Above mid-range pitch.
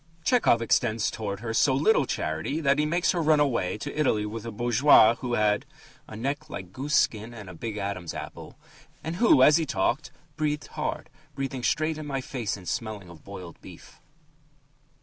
No: low, 120 Hz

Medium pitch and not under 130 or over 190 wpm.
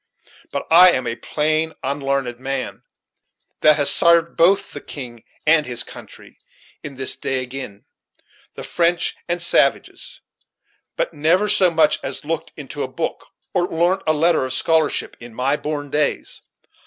Yes: medium, 150 Hz; average, 155 wpm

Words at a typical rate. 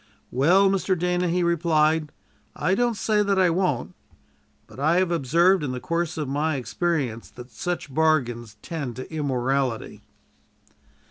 Yes: average, 145 wpm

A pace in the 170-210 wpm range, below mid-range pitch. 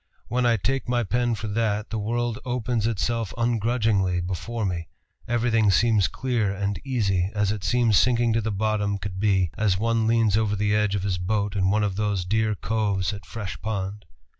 Yes: average, 190 wpm; low, 105 Hz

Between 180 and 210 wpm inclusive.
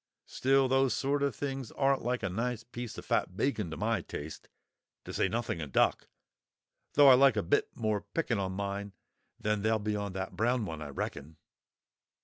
Yes: average, 190 wpm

